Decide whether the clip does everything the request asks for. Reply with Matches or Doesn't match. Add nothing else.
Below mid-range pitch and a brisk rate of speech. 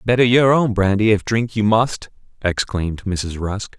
Doesn't match